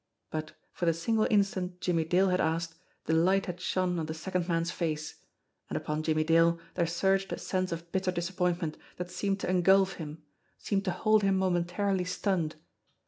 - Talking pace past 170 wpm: Yes, average, 195 wpm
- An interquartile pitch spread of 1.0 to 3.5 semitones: Yes, narrow, 2.4 semitones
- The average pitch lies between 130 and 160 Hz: No, medium, 180 Hz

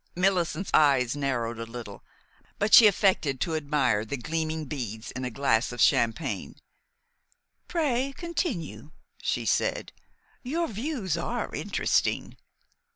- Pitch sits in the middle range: Yes, medium, 155 Hz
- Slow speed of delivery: Yes, slow, 120 wpm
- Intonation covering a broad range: Yes, wide, 8.6 semitones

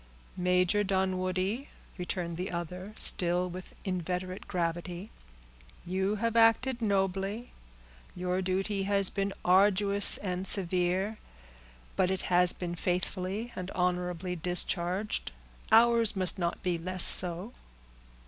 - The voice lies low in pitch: No, medium, 185 Hz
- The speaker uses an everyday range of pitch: No, narrow, 1.9 semitones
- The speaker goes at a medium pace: No, slow, 110 wpm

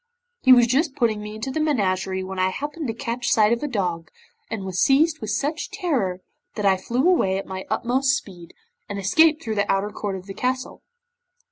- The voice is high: Yes, high, 220 Hz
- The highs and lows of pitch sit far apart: Yes, wide, 6.0 semitones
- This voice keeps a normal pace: No, fast, 210 wpm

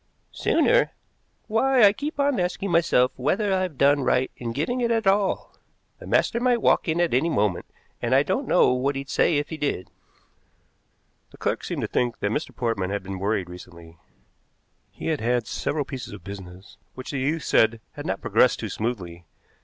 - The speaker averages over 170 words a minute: Yes, average, 190 wpm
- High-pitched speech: No, medium, 140 Hz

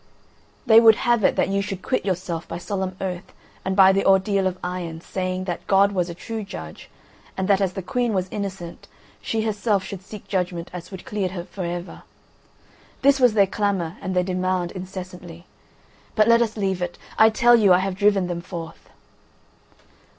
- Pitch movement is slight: Yes, narrow, 2.2 semitones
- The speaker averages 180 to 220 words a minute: Yes, average, 195 wpm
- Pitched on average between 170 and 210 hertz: Yes, high, 190 Hz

